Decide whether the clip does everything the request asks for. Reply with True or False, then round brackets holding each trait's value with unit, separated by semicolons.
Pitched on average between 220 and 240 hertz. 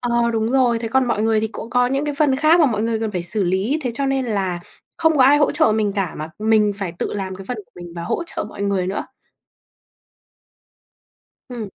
True (225 Hz)